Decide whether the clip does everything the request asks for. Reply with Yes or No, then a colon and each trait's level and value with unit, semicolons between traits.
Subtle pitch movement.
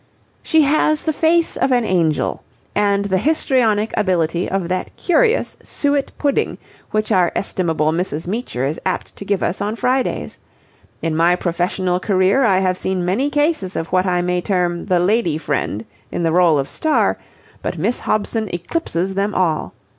No: average, 5.0 semitones